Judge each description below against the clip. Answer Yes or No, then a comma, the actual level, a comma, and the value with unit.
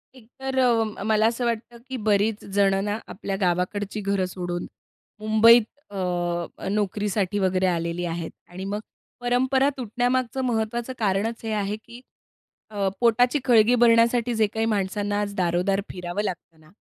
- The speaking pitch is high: Yes, high, 210 Hz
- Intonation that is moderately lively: Yes, average, 3.6 semitones